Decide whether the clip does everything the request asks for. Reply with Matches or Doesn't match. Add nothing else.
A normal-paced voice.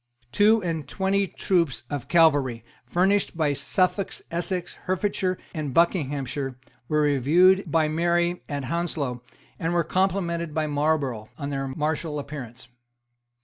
Doesn't match